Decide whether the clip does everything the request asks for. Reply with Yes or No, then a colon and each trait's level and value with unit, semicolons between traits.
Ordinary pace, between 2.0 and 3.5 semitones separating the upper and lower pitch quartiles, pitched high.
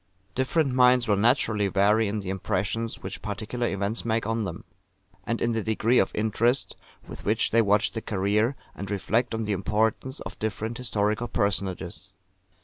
No: average, 165 wpm; narrow, 2.5 semitones; low, 110 Hz